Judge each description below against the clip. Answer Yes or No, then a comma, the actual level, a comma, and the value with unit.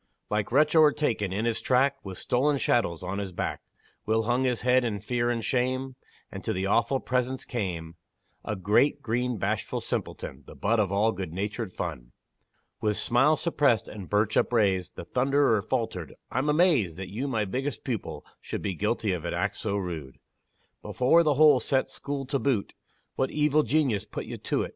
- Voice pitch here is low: Yes, low, 115 Hz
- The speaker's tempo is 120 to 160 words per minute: No, average, 180 wpm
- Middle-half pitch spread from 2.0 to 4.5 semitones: No, average, 5.0 semitones